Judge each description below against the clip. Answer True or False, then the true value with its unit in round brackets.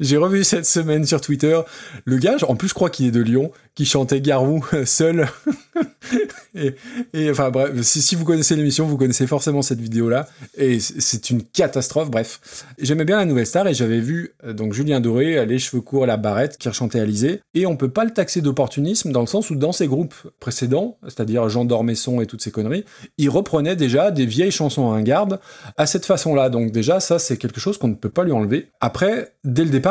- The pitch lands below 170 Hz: True (140 Hz)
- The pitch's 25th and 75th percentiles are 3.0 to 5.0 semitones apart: False (5.4 semitones)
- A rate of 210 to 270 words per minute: True (220 wpm)